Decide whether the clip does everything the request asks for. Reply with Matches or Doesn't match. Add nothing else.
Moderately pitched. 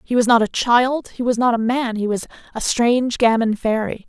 Doesn't match